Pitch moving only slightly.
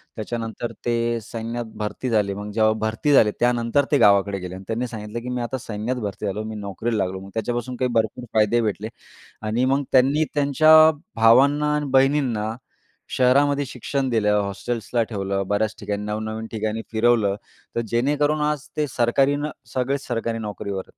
No: average, 3.7 semitones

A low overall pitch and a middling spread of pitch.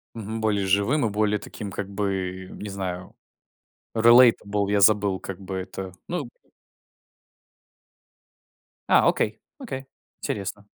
No: low, 100 Hz; narrow, 2.3 semitones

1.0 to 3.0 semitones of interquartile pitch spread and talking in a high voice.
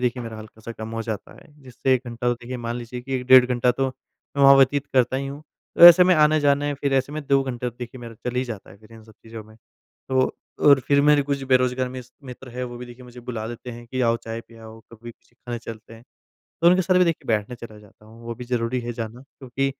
No: narrow, 2.6 semitones; low, 125 Hz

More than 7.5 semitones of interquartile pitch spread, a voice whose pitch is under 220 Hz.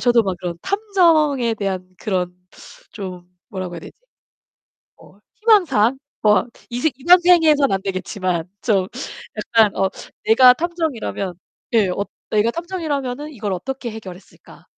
No: wide, 7.9 semitones; high, 225 Hz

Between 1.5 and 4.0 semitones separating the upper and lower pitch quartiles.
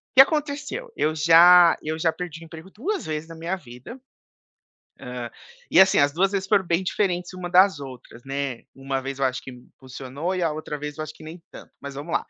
No: average, 4.8 semitones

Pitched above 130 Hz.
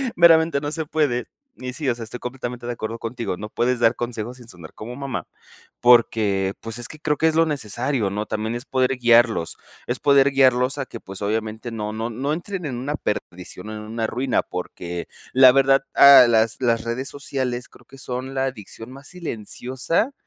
No: low, 125 Hz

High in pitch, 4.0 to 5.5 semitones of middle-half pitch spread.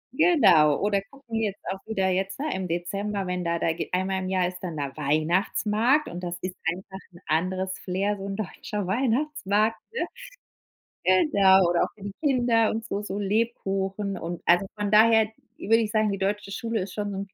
No: high, 195 Hz; average, 3.0 semitones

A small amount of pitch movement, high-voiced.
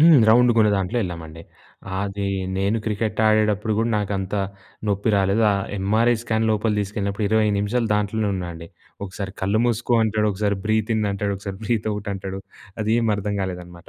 No: narrow, 2.1 semitones; low, 105 Hz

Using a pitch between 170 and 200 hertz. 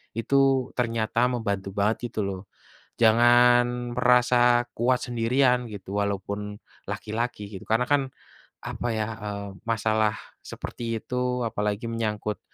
No: low, 115 Hz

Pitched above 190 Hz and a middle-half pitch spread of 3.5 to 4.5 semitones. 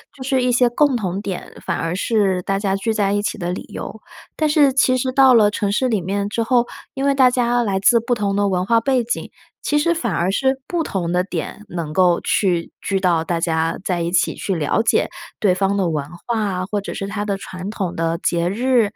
No: high, 200 Hz; average, 5.0 semitones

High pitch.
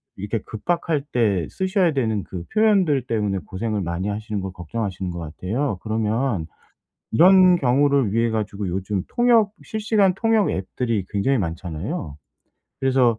No: low, 110 Hz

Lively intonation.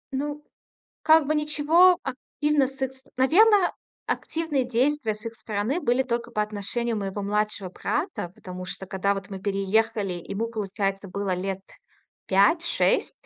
Yes: wide, 6.8 semitones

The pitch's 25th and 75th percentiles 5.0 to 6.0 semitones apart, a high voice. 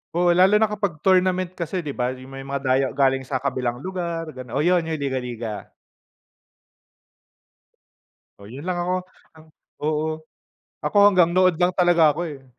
No: average, 5.3 semitones; medium, 155 Hz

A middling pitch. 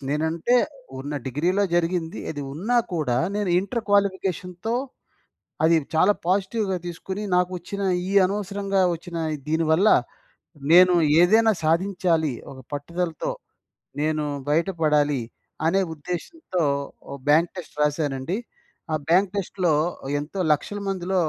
Yes: medium, 175 Hz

